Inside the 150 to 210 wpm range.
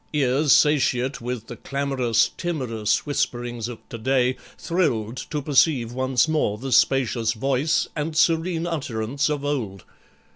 No: slow, 135 wpm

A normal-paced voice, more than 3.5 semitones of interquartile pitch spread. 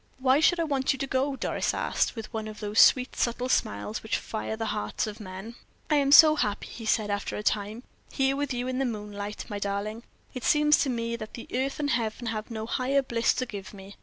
No: fast, 230 wpm; average, 4.0 semitones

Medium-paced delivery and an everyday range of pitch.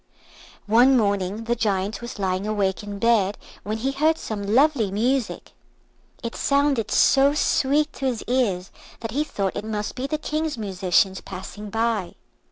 Yes: average, 160 wpm; average, 4.8 semitones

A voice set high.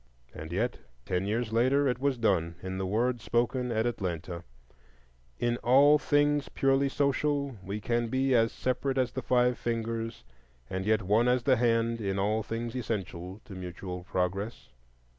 No: low, 115 Hz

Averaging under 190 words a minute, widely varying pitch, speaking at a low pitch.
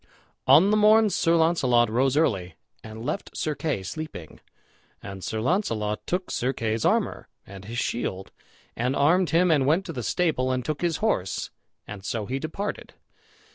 Yes: average, 170 wpm; wide, 7.3 semitones; low, 130 Hz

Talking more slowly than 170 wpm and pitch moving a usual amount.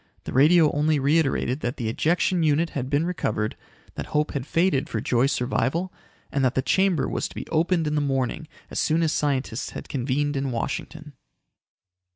No: average, 185 wpm; average, 3.4 semitones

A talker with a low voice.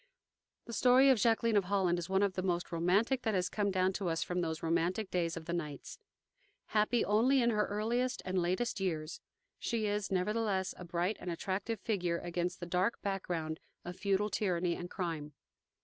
No: high, 190 Hz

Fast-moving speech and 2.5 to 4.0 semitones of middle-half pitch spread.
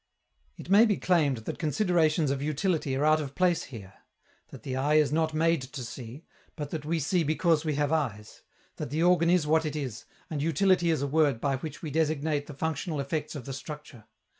Yes: fast, 215 wpm; average, 2.8 semitones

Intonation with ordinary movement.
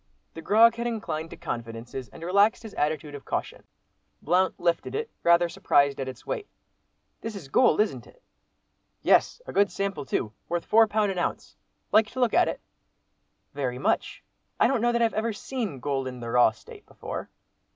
No: wide, 8.2 semitones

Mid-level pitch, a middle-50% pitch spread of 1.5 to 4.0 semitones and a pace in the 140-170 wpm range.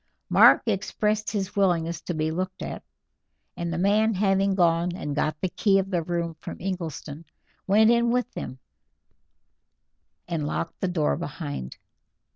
Yes: medium, 180 Hz; average, 3.2 semitones; average, 150 wpm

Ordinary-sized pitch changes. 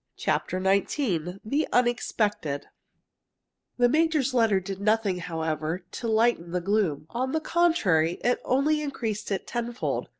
No: wide, 5.8 semitones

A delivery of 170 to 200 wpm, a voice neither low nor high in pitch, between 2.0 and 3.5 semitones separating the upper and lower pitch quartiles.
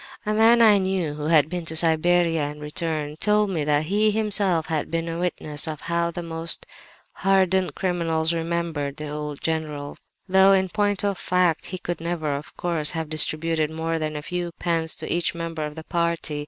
Yes: average, 195 wpm; medium, 165 Hz; narrow, 2.6 semitones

